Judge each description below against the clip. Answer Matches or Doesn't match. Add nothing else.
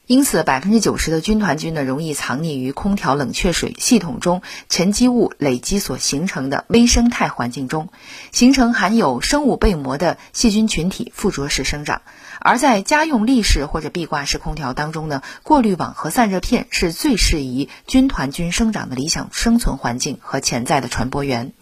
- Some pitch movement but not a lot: Doesn't match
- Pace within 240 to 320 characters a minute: Matches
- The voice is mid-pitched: Matches